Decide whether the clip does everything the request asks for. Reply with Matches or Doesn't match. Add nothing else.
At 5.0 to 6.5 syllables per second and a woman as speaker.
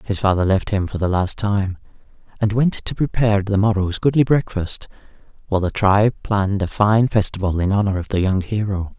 Doesn't match